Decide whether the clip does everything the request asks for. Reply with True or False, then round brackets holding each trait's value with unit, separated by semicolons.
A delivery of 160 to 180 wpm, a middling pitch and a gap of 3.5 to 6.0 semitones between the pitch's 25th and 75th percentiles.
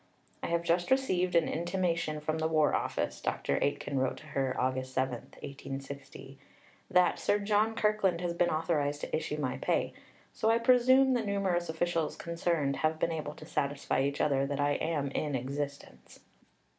True (170 wpm; 155 Hz; 4.1 semitones)